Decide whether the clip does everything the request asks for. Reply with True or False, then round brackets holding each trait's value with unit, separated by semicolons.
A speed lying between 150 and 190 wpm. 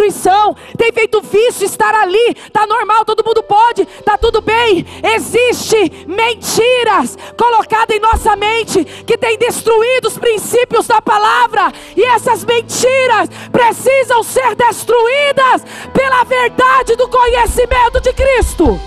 False (120 wpm)